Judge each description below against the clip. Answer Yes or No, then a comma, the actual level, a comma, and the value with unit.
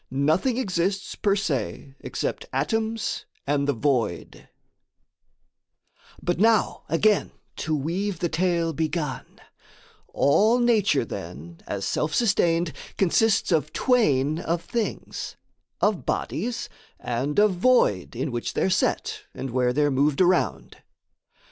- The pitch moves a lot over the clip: Yes, wide, 6.6 semitones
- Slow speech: Yes, slow, 115 wpm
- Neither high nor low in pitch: Yes, medium, 165 Hz